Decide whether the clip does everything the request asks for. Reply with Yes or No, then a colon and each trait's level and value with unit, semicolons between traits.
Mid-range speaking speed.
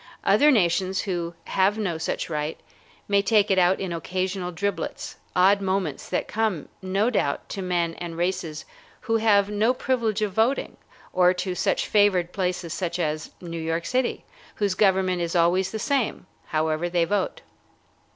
Yes: average, 160 wpm